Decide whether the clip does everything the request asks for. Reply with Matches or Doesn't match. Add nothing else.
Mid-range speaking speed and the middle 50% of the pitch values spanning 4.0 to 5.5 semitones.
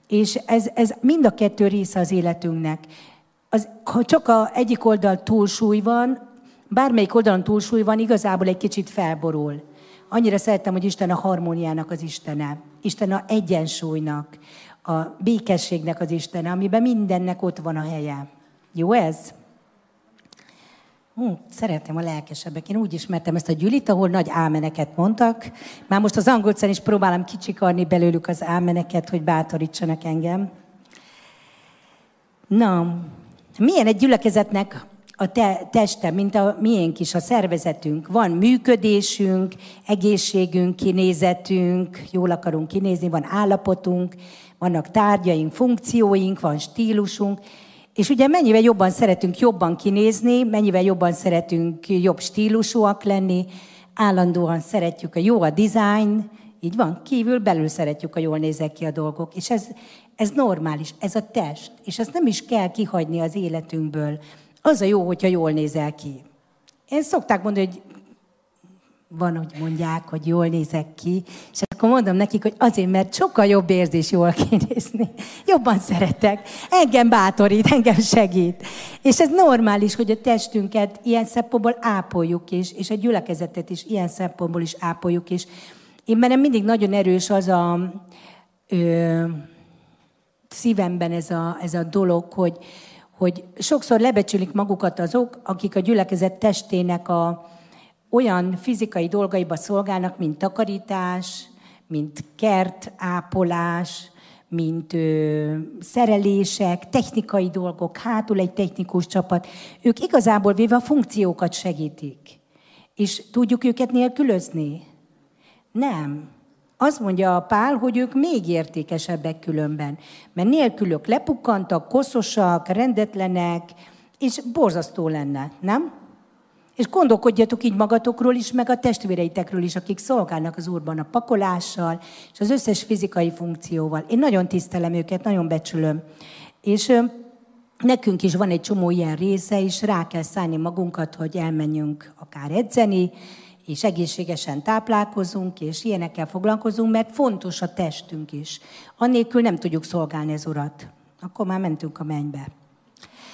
Matches